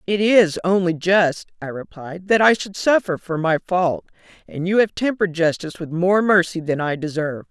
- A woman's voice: Yes, female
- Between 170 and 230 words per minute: Yes, average, 190 wpm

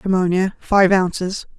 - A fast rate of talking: No, slow, 115 wpm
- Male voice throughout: No, female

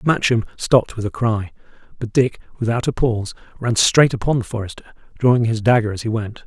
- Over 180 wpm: Yes, average, 195 wpm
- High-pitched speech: No, low, 115 Hz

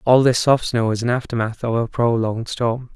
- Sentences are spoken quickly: Yes, fast, 225 wpm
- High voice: No, low, 120 Hz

